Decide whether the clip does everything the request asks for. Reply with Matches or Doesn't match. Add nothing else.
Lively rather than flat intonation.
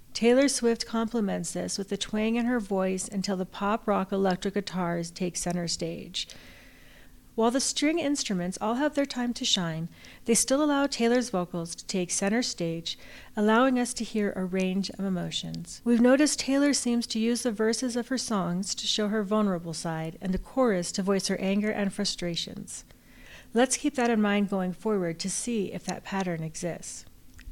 Doesn't match